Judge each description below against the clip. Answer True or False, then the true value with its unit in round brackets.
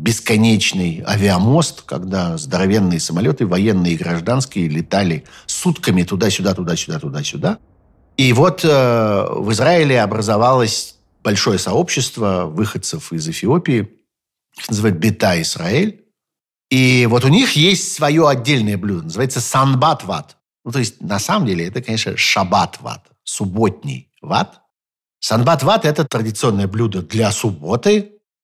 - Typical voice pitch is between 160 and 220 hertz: False (115 Hz)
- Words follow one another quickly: False (115 wpm)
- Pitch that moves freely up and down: True (6.9 semitones)